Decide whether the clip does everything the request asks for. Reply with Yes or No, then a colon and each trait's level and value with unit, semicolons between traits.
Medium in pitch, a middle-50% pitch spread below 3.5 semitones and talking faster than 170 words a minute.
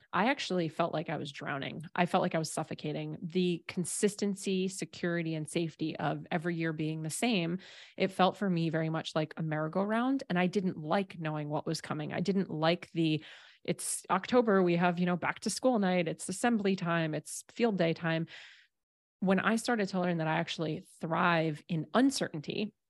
Yes: medium, 175 Hz; average, 3.1 semitones; average, 190 wpm